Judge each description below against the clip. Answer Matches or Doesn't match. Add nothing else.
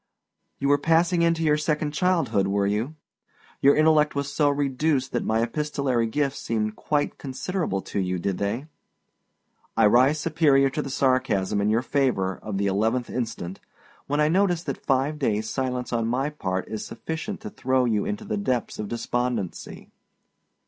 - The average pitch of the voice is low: Matches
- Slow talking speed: Doesn't match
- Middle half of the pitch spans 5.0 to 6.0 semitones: Matches